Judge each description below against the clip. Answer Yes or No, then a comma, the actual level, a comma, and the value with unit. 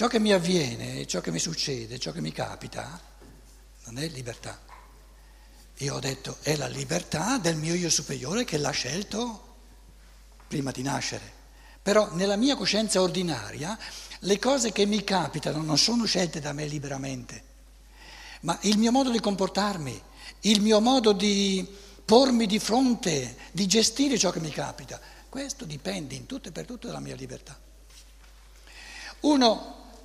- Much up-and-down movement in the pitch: Yes, wide, 7.2 semitones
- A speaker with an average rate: Yes, average, 155 wpm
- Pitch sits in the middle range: No, high, 195 Hz